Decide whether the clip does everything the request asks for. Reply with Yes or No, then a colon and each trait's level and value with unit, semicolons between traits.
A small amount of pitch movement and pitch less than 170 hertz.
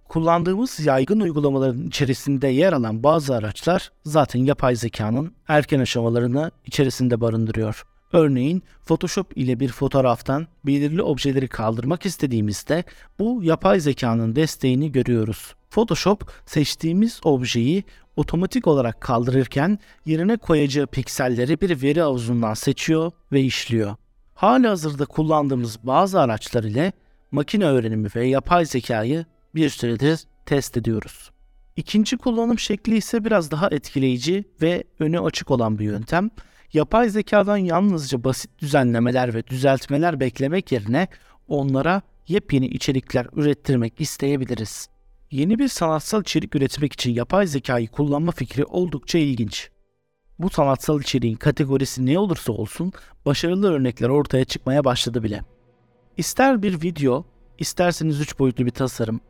No: average, 5.2 semitones; medium, 140 Hz